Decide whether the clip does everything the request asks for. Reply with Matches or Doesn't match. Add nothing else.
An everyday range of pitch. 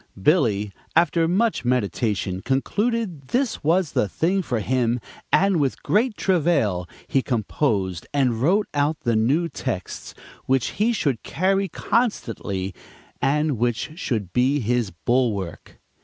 Doesn't match